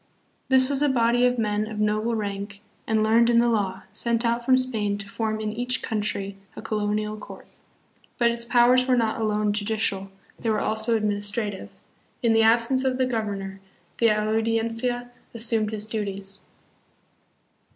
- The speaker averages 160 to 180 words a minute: Yes, average, 165 wpm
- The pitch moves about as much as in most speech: No, narrow, 2.1 semitones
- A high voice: Yes, high, 220 Hz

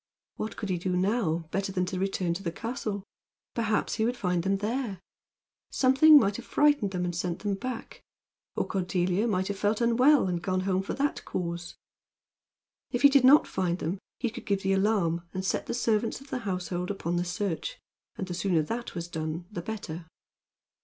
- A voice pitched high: Yes, high, 195 Hz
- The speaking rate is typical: Yes, average, 195 wpm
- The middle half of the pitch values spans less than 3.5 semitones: No, average, 4.3 semitones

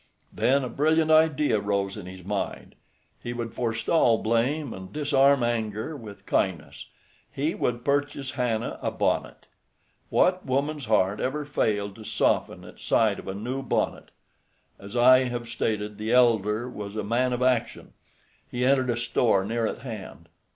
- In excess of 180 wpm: No, average, 155 wpm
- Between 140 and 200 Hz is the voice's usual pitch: No, low, 120 Hz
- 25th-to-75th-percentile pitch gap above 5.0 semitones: No, average, 4.2 semitones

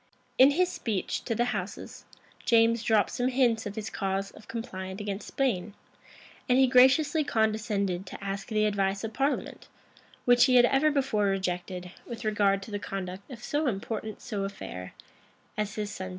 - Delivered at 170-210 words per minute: Yes, average, 175 wpm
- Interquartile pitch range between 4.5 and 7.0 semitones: No, average, 3.9 semitones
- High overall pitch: Yes, high, 215 Hz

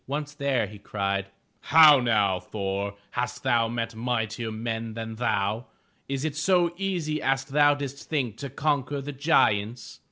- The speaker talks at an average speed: Yes, average, 155 wpm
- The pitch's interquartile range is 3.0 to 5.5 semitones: Yes, average, 4.7 semitones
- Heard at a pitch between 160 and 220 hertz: No, low, 125 Hz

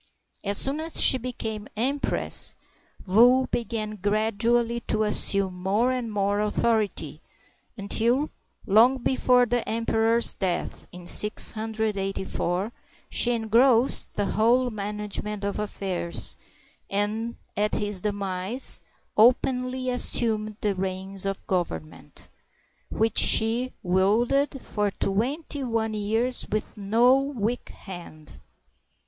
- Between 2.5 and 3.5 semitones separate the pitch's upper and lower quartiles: Yes, average, 3.2 semitones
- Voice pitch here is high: Yes, high, 220 Hz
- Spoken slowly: Yes, slow, 105 wpm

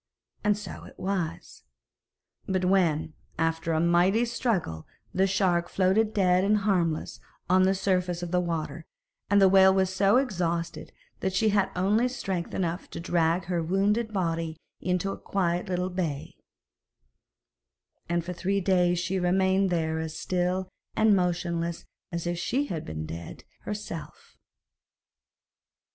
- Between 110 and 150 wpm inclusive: Yes, average, 140 wpm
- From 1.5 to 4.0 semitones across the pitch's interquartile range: Yes, narrow, 2.4 semitones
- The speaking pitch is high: No, medium, 180 Hz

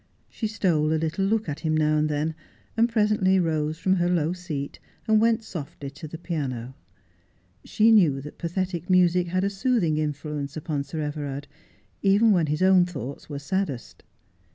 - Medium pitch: Yes, medium, 165 Hz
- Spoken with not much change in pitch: No, average, 4.2 semitones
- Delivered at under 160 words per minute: No, average, 175 wpm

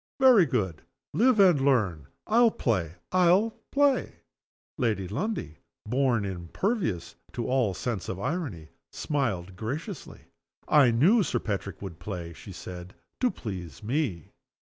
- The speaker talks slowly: Yes, slow, 125 wpm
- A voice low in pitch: Yes, low, 115 Hz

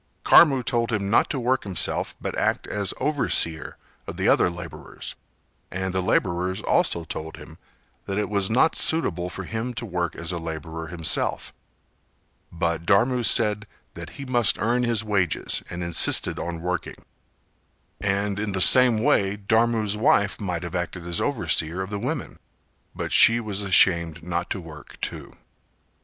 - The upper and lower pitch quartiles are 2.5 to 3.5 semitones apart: No, average, 4.5 semitones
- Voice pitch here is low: Yes, low, 100 Hz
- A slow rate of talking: No, average, 160 wpm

